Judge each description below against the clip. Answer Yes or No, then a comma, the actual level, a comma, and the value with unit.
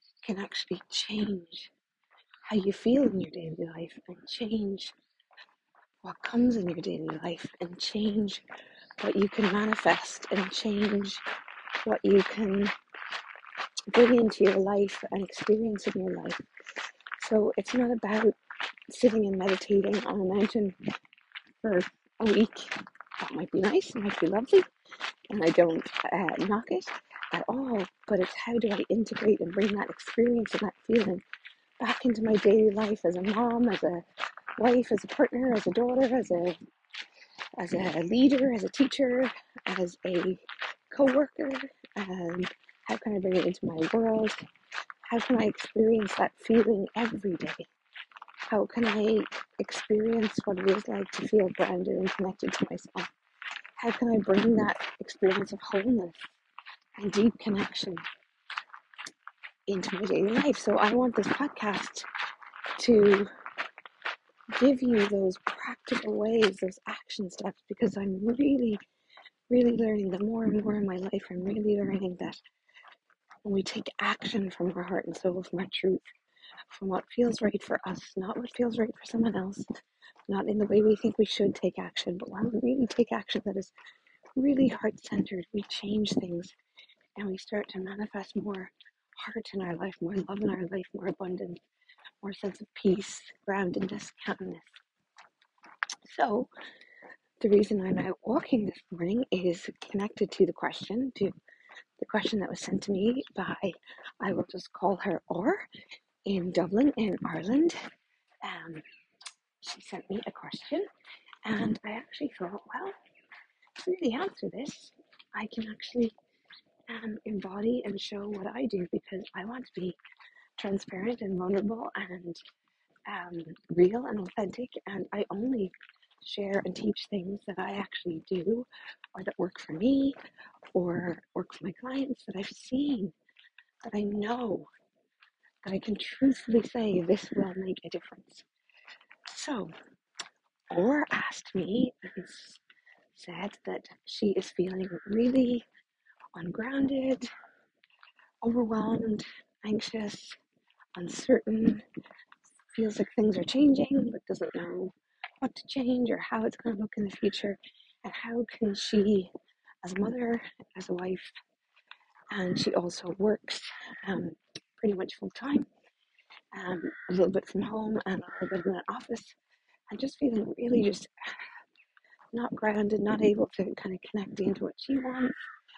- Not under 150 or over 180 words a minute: Yes, average, 155 wpm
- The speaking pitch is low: No, high, 210 Hz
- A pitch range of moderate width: Yes, average, 3.8 semitones